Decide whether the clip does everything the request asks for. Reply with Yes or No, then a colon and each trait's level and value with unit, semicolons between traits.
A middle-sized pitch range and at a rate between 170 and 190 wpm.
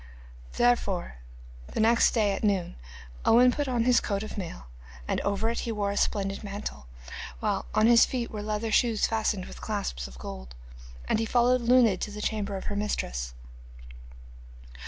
Yes: average, 3.0 semitones; average, 175 wpm